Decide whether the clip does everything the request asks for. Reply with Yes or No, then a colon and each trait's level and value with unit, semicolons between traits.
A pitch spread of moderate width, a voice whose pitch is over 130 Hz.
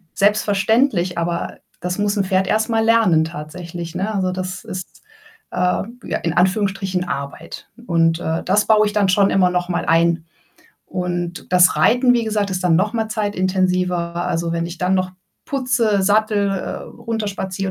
Yes: average, 3.0 semitones; medium, 185 Hz